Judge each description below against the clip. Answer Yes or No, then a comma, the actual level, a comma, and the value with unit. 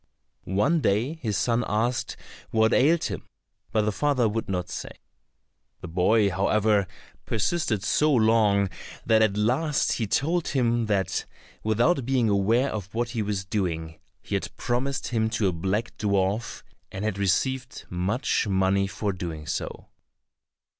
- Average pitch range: Yes, average, 3.7 semitones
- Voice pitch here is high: No, low, 110 Hz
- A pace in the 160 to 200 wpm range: No, average, 145 wpm